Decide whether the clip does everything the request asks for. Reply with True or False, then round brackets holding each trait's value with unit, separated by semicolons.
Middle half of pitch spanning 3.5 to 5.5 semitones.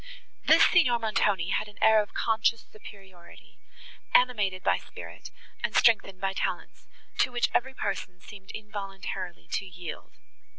False (2.9 semitones)